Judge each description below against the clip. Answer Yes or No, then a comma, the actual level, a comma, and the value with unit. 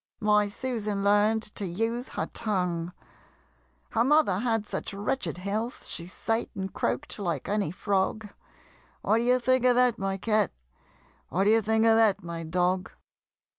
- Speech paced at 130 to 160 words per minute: Yes, average, 150 wpm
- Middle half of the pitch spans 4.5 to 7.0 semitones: No, average, 2.9 semitones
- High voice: Yes, high, 210 Hz